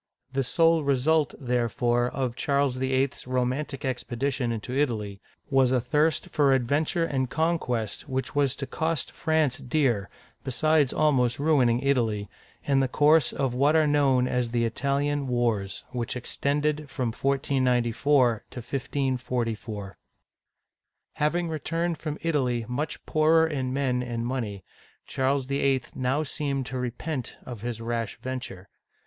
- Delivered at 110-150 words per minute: Yes, average, 140 wpm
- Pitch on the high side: No, low, 130 Hz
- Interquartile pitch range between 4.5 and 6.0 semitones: No, average, 3.2 semitones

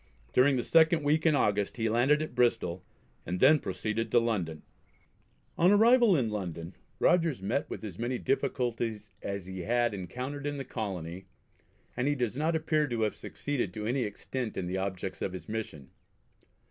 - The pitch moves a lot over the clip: Yes, wide, 6.6 semitones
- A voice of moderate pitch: No, low, 115 Hz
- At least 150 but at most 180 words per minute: Yes, average, 175 wpm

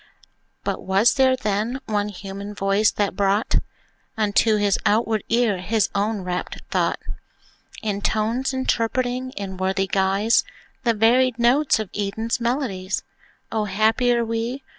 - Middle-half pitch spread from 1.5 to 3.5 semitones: Yes, average, 3.0 semitones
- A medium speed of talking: No, slow, 130 wpm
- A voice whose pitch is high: Yes, high, 215 Hz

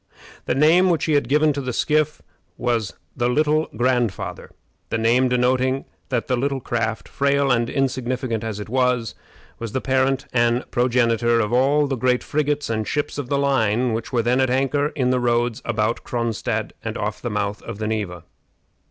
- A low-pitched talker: Yes, low, 125 Hz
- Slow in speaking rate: No, average, 185 wpm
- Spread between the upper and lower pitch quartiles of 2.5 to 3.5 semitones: Yes, average, 2.8 semitones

